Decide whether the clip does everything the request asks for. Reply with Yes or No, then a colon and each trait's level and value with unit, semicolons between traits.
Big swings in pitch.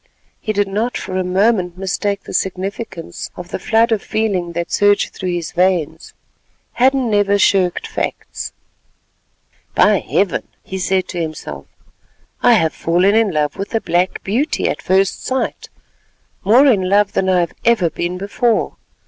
No: average, 3.2 semitones